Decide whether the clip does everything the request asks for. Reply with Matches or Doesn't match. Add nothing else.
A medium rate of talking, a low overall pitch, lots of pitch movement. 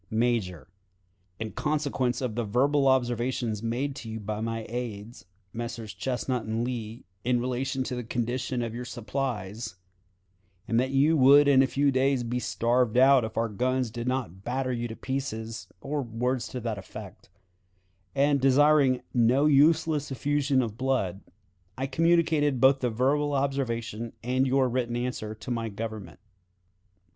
Doesn't match